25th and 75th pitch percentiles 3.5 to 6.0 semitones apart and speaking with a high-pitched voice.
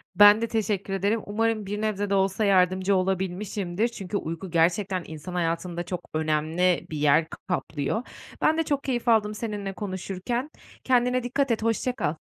Yes: average, 3.8 semitones; high, 195 Hz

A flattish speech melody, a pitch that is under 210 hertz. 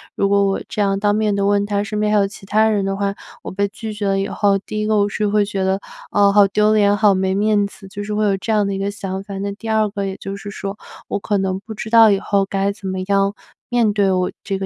Yes: narrow, 1.2 semitones; high, 200 Hz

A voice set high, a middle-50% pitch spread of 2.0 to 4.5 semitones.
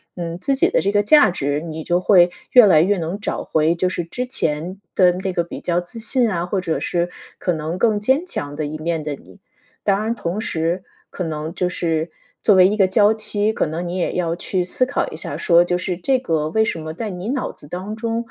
No: medium, 180 Hz; average, 4.1 semitones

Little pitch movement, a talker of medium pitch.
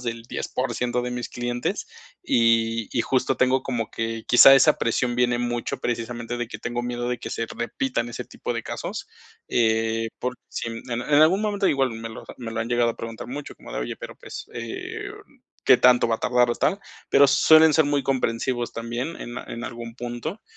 No: narrow, 2.2 semitones; low, 120 Hz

